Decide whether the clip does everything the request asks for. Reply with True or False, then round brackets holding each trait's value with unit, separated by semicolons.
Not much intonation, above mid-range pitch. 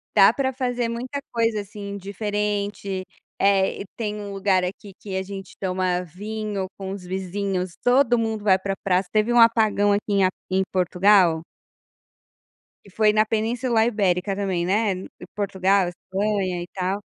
True (2.2 semitones; 200 Hz)